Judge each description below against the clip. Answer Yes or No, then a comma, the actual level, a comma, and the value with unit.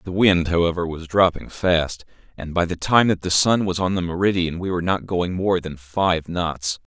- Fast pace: Yes, fast, 215 wpm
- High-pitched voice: No, very low, 90 Hz